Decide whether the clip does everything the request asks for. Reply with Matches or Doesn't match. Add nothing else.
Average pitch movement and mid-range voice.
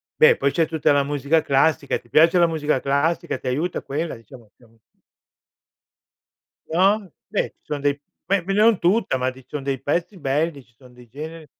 Matches